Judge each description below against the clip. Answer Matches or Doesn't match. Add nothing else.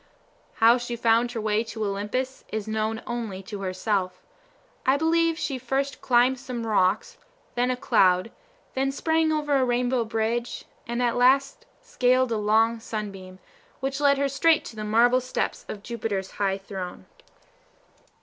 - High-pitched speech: Matches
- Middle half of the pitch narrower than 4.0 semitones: Matches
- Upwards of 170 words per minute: Doesn't match